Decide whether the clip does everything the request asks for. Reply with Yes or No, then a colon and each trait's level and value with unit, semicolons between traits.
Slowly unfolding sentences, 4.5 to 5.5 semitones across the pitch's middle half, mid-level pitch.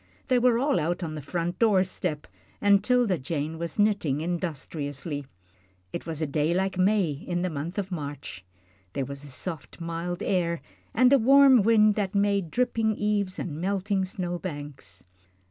No: average, 170 wpm; average, 4.8 semitones; medium, 180 Hz